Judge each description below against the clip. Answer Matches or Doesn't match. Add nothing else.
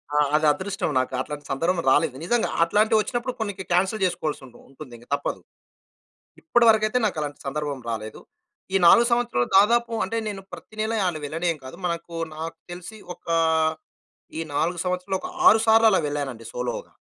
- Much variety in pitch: Matches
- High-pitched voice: Doesn't match